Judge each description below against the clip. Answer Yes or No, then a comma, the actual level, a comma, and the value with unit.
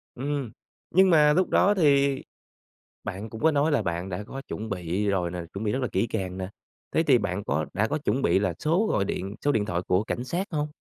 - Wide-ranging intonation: Yes, wide, 7.5 semitones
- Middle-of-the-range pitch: No, low, 110 Hz